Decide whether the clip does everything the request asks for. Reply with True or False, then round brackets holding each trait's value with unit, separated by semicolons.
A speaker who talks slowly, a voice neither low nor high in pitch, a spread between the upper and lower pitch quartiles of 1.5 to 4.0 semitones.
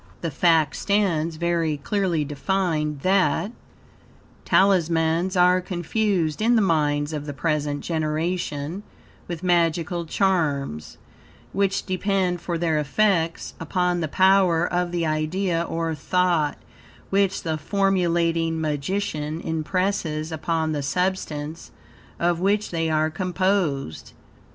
True (110 wpm; 170 Hz; 3.2 semitones)